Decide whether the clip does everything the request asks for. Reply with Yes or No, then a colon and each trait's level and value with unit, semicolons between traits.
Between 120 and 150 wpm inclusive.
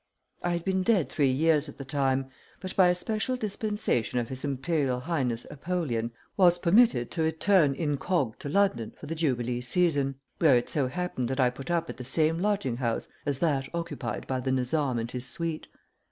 No: average, 195 wpm